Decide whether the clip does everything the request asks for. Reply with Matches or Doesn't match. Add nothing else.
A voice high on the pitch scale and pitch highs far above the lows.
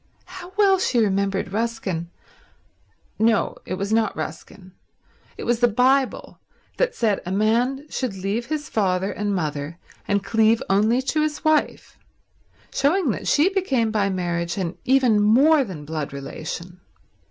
Matches